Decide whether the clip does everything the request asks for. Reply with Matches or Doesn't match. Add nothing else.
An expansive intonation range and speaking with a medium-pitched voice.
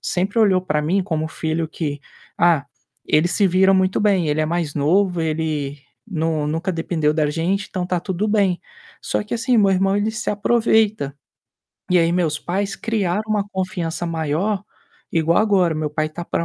Doesn't match